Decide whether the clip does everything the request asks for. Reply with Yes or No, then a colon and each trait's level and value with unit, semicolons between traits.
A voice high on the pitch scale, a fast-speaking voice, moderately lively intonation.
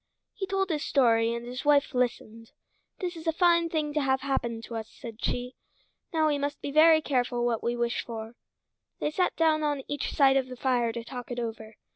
Yes: very high, 265 Hz; fast, 220 wpm; average, 4.6 semitones